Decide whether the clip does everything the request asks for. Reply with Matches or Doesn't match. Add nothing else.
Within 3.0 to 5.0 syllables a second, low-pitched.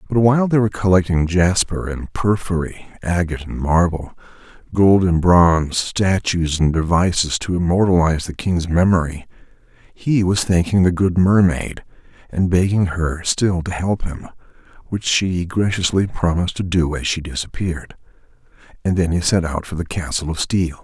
Matches